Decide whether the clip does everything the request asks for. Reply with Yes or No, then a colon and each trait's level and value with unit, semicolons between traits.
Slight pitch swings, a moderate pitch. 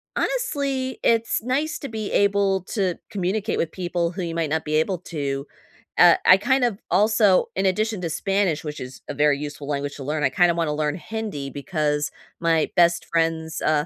No: average, 5.3 semitones; medium, 175 Hz